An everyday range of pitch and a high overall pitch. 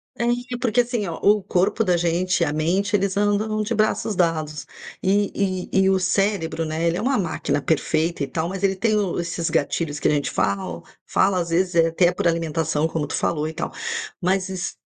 No: average, 3.8 semitones; medium, 180 Hz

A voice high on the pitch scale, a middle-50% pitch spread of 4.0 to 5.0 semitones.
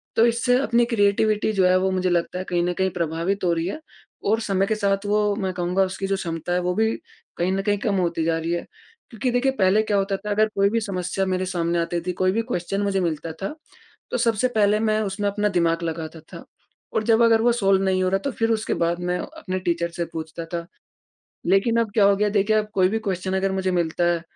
No: high, 195 Hz; average, 3.1 semitones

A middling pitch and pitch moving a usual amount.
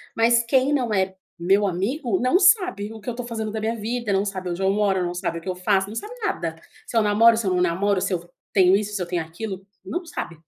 No: high, 205 Hz; average, 3.8 semitones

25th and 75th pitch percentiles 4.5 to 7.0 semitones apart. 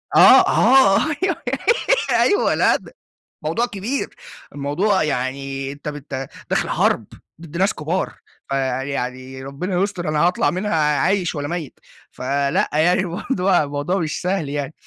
Yes: average, 5.2 semitones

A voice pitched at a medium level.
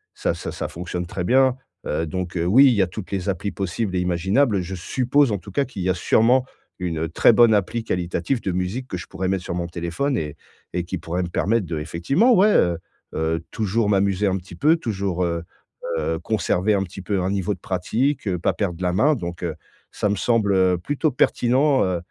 No: very low, 95 Hz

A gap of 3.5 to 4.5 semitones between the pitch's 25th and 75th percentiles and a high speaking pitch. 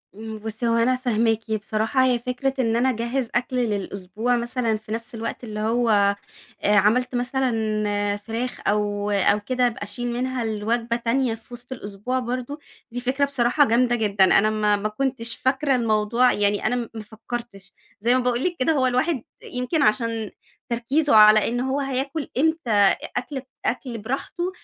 No: average, 2.8 semitones; high, 235 Hz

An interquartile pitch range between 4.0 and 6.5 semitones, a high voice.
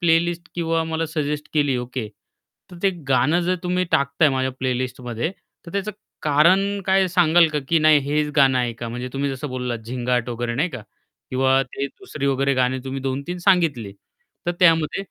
No: average, 4.5 semitones; medium, 140 Hz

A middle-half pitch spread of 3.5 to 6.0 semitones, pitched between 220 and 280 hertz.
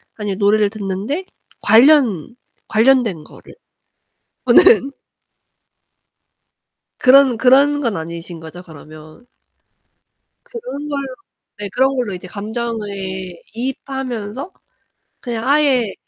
Yes: average, 5.2 semitones; high, 235 Hz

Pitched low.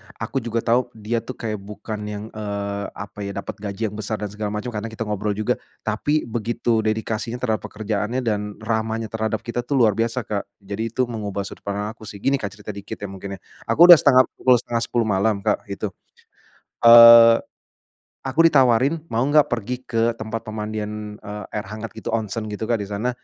Yes: low, 110 Hz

